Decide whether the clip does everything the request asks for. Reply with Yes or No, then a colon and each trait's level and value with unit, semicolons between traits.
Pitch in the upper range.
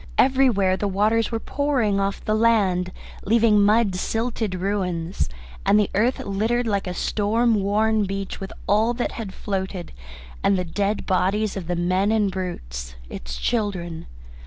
Yes: high, 200 Hz